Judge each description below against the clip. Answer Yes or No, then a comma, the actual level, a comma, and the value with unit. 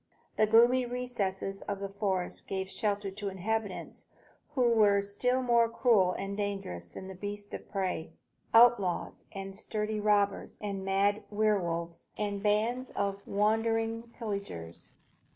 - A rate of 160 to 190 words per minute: No, slow, 135 wpm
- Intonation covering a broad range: No, narrow, 2.4 semitones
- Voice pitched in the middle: No, high, 205 Hz